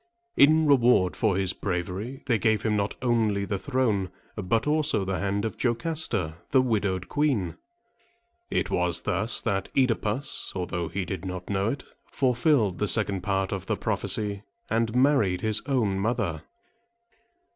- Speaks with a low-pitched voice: Yes, low, 105 Hz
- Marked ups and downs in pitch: No, average, 4.4 semitones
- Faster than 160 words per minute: No, average, 150 wpm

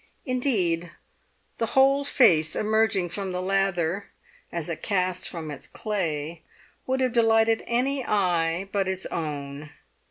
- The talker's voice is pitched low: No, high, 190 Hz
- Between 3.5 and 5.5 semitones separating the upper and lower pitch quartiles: Yes, average, 5.1 semitones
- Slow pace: Yes, slow, 130 wpm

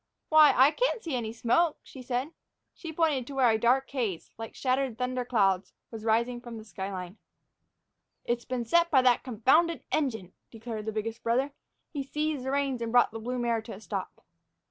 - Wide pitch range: No, average, 3.5 semitones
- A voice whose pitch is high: Yes, high, 245 Hz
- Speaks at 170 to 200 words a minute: Yes, average, 190 wpm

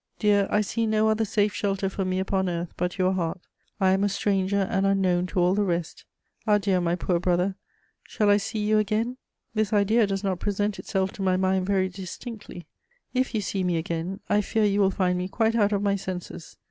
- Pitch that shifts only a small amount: Yes, narrow, 2.1 semitones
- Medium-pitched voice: No, high, 195 Hz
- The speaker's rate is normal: No, fast, 215 wpm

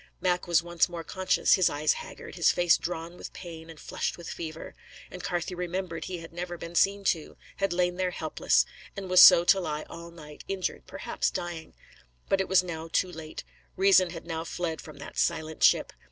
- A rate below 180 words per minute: No, average, 200 wpm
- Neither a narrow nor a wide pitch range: No, narrow, 2.0 semitones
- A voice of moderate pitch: Yes, medium, 175 Hz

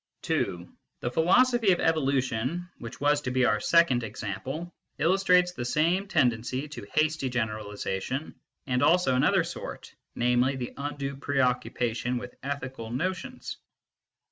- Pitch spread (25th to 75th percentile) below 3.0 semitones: No, average, 5.1 semitones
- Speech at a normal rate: No, slow, 125 wpm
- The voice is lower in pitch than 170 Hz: Yes, low, 135 Hz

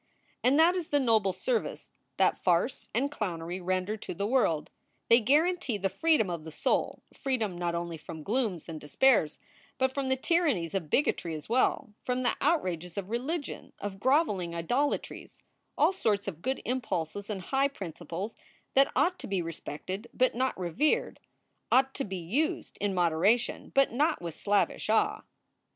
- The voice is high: Yes, high, 215 Hz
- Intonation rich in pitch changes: Yes, wide, 7.2 semitones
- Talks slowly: No, average, 165 wpm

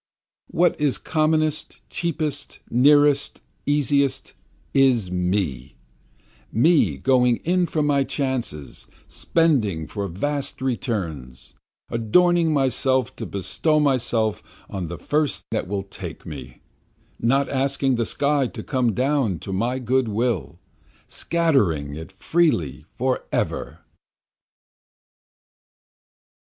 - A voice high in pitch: No, low, 130 Hz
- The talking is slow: Yes, slow, 100 wpm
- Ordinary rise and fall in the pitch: No, wide, 6.9 semitones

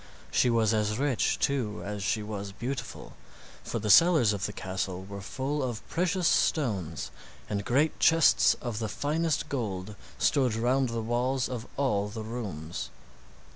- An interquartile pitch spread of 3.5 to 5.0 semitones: Yes, average, 4.7 semitones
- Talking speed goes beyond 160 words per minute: No, average, 155 wpm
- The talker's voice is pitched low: Yes, low, 115 Hz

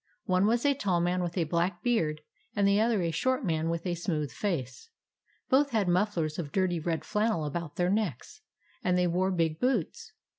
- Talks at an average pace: Yes, average, 195 wpm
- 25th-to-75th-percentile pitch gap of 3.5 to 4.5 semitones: Yes, average, 4.0 semitones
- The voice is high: No, medium, 180 Hz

